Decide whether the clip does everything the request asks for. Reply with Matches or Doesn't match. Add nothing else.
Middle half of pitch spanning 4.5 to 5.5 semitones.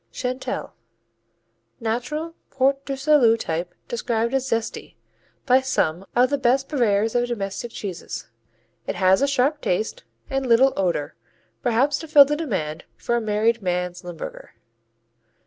Matches